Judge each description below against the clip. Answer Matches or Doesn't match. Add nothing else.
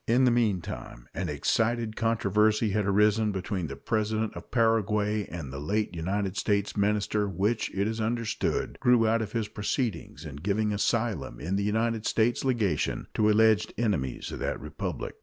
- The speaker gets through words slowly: Doesn't match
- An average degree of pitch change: Doesn't match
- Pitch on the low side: Matches